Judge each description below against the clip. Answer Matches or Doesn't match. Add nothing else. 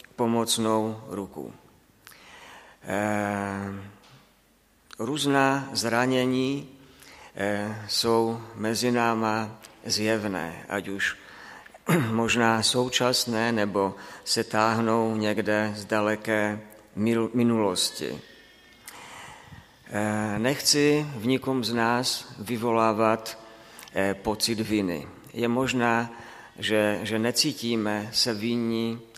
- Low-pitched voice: Matches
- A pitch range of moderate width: Doesn't match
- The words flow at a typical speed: Doesn't match